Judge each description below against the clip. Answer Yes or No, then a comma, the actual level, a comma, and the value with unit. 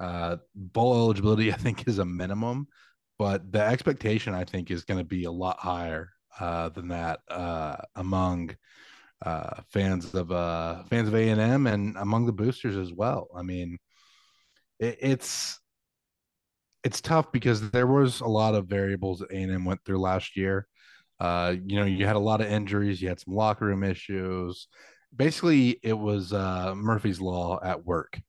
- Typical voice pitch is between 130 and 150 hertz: No, low, 100 Hz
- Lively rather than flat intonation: No, average, 3.4 semitones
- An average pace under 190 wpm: Yes, average, 170 wpm